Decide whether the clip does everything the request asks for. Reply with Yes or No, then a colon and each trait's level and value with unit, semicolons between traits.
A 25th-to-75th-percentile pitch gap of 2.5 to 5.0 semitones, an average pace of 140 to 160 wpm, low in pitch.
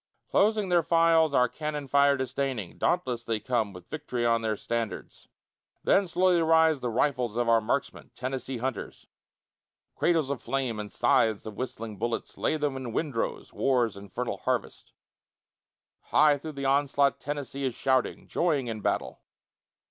Yes: average, 4.2 semitones; average, 150 wpm; low, 130 Hz